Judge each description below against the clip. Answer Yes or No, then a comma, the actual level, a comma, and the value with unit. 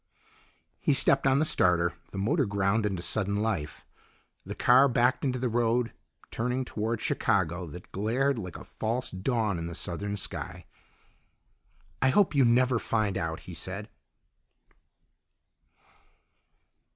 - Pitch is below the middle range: Yes, low, 110 Hz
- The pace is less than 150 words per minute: Yes, slow, 135 wpm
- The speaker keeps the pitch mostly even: No, average, 5.0 semitones